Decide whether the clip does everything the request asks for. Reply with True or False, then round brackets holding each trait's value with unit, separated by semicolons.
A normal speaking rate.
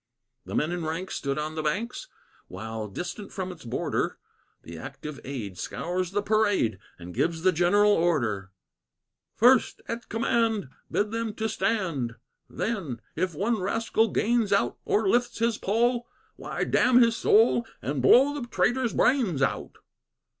True (150 wpm)